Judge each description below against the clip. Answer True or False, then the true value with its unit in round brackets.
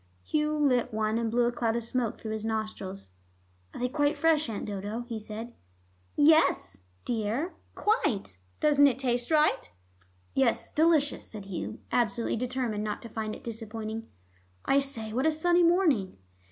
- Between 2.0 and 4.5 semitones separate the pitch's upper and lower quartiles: False (4.9 semitones)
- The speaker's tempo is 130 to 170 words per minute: True (160 wpm)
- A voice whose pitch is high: True (235 Hz)